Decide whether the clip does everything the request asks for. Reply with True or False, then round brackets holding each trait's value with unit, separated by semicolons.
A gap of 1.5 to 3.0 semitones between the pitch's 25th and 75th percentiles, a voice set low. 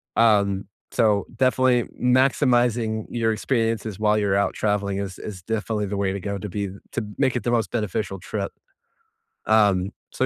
True (2.7 semitones; 105 Hz)